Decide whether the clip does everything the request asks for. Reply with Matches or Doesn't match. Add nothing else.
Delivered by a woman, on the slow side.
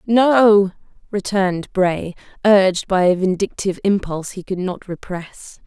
Matches